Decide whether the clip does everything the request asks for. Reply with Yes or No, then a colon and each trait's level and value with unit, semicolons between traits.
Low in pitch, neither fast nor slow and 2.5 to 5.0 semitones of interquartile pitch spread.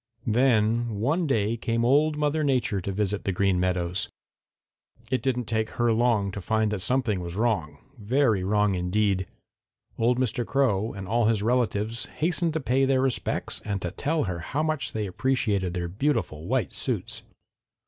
Yes: low, 110 Hz; average, 170 wpm; average, 4.6 semitones